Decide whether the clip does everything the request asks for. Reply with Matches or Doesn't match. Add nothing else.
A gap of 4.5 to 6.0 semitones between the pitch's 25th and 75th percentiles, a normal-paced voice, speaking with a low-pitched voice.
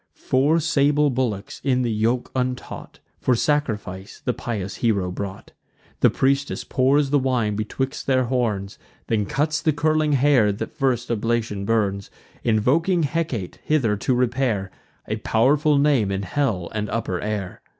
Matches